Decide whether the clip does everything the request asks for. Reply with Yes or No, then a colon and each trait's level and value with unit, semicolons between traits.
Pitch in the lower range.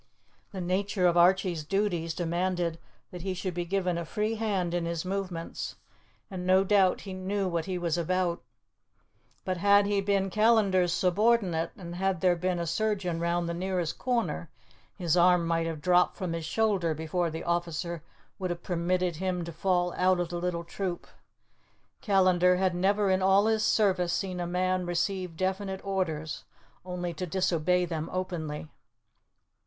No: medium, 180 Hz